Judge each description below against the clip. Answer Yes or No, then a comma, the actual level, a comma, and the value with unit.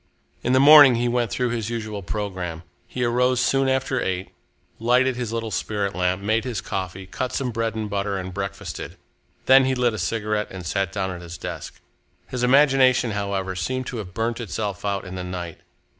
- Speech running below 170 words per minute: No, average, 195 wpm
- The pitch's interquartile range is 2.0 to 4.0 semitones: No, average, 4.6 semitones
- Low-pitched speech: Yes, low, 110 Hz